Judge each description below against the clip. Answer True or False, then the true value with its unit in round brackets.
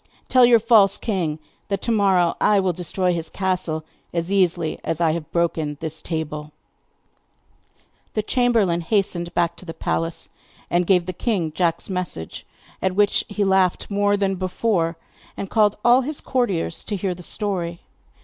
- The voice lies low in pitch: False (185 Hz)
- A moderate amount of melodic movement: True (3.3 semitones)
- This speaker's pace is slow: False (160 wpm)